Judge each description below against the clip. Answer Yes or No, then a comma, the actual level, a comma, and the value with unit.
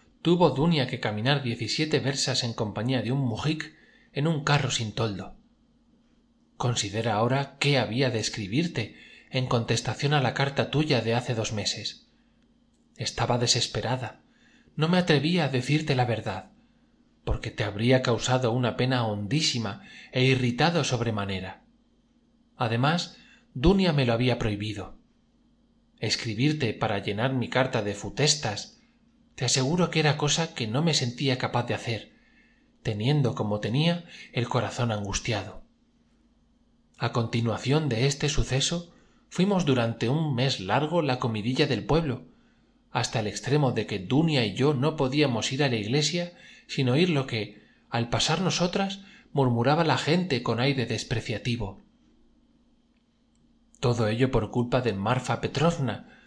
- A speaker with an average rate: Yes, average, 140 wpm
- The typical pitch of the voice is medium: No, low, 130 Hz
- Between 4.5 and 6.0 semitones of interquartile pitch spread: Yes, average, 5.1 semitones